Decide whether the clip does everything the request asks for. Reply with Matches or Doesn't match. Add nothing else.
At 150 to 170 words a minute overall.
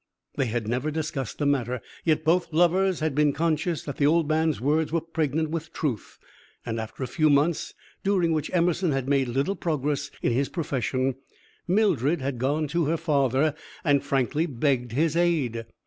Doesn't match